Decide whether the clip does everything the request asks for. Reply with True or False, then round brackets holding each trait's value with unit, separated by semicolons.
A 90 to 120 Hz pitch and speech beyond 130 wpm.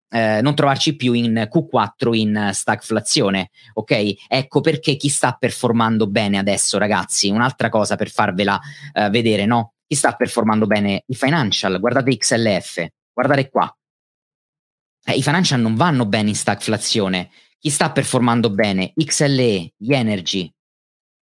True (115 Hz; 140 wpm)